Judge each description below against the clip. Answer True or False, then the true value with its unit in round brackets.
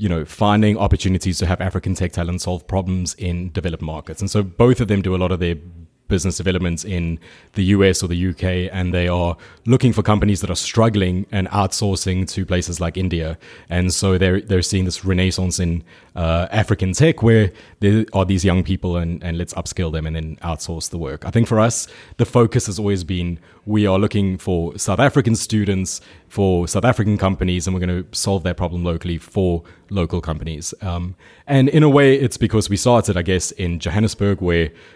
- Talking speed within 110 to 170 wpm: False (205 wpm)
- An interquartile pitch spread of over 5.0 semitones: False (2.7 semitones)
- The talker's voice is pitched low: True (95 Hz)